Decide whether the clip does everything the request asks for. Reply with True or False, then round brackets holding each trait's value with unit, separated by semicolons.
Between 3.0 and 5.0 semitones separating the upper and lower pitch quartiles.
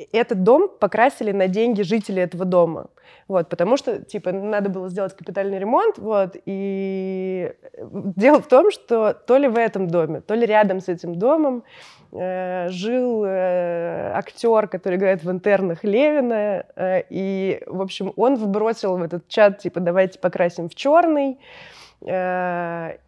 True (3.8 semitones)